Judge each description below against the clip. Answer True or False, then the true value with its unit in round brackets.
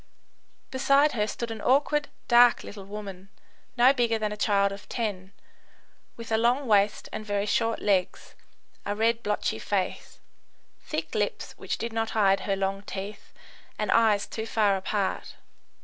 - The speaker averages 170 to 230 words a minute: False (155 wpm)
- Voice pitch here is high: True (210 Hz)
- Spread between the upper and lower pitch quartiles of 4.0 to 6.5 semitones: False (2.6 semitones)